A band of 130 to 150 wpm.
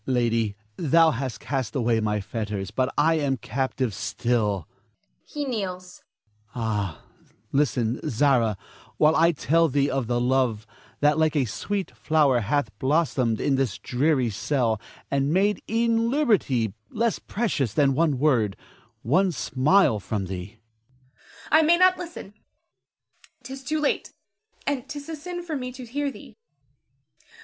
Yes: average, 140 wpm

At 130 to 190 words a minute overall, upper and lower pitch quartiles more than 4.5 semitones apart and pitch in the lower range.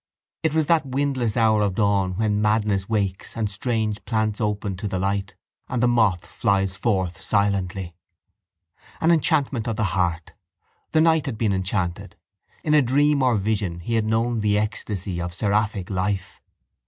No: average, 165 wpm; average, 3.4 semitones; low, 105 Hz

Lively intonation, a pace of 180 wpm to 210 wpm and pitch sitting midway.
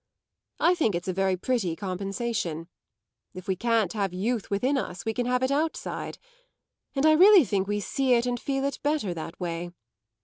No: wide, 6.0 semitones; average, 190 wpm; high, 220 Hz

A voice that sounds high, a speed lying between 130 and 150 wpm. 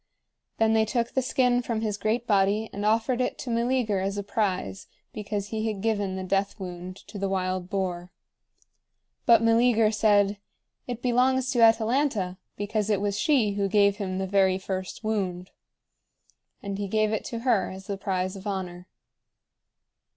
No: high, 205 Hz; average, 170 wpm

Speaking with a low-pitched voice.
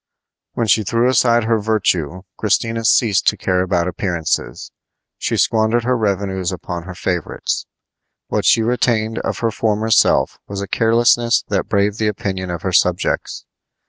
Yes: low, 105 Hz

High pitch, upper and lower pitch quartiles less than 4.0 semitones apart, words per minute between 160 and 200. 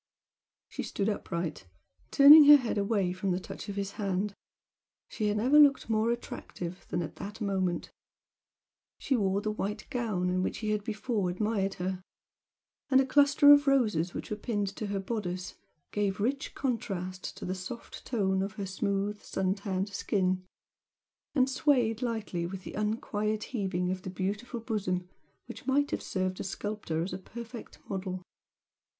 Yes: high, 205 Hz; average, 3.6 semitones; average, 165 wpm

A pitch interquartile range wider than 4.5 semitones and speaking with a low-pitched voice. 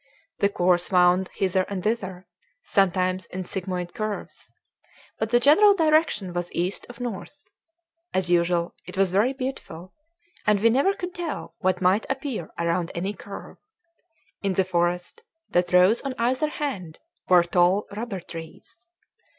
No: average, 5.0 semitones; high, 190 Hz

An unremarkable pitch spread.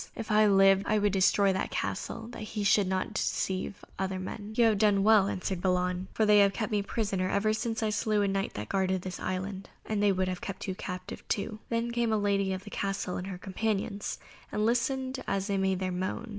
No: narrow, 2.2 semitones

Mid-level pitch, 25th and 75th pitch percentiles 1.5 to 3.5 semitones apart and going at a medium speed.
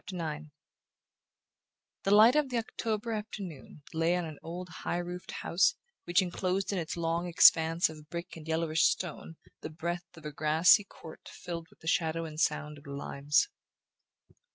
Yes: medium, 170 Hz; narrow, 2.4 semitones; average, 170 wpm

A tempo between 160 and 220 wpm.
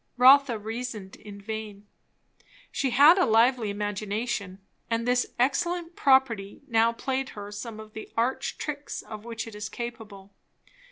No: average, 145 wpm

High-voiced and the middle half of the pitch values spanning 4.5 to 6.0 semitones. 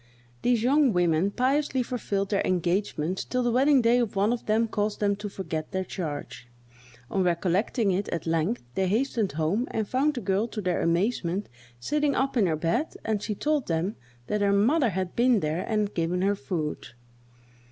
Yes: high, 205 Hz; average, 5.2 semitones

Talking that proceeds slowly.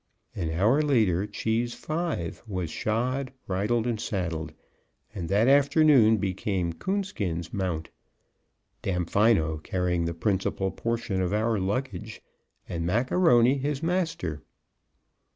Yes: slow, 115 wpm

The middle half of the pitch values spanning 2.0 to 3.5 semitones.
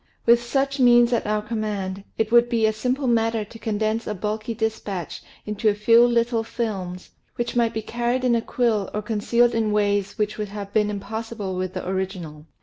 Yes: narrow, 2.5 semitones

